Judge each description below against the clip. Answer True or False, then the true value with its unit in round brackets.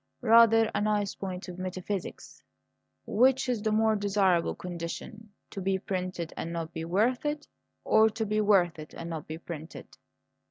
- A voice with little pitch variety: False (3.9 semitones)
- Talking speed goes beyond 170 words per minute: False (165 wpm)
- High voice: True (200 Hz)